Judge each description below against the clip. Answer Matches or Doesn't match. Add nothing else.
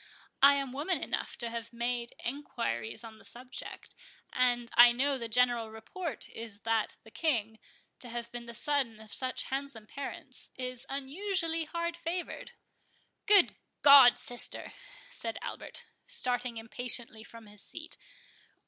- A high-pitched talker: Matches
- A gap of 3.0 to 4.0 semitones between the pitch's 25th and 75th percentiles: Matches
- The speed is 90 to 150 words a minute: Matches